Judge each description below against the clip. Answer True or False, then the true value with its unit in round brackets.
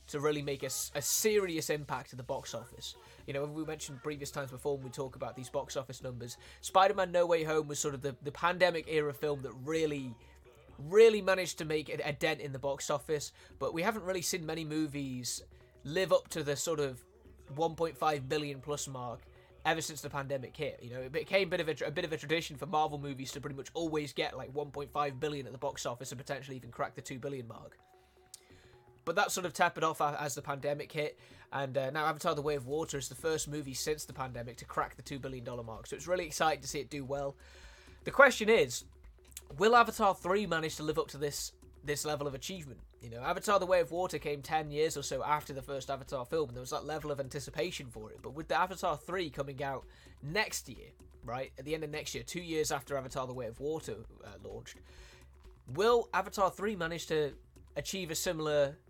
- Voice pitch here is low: False (145 Hz)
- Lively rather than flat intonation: False (2.8 semitones)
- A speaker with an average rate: False (230 wpm)